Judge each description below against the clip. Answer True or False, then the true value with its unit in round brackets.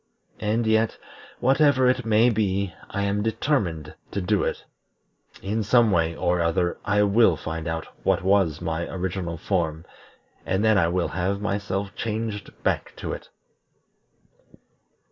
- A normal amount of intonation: True (4.0 semitones)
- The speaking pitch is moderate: False (100 Hz)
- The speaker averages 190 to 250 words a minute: False (145 wpm)